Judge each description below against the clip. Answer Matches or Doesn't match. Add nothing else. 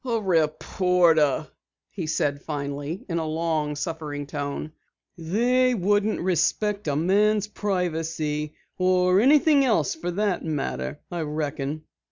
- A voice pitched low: Doesn't match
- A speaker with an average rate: Doesn't match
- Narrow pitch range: Doesn't match